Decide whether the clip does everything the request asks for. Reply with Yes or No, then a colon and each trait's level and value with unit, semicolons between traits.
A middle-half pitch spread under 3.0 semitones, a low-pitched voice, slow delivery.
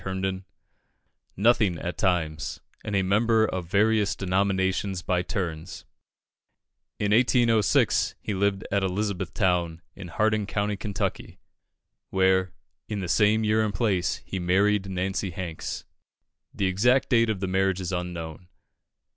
Yes: narrow, 2.4 semitones; very low, 95 Hz; slow, 130 wpm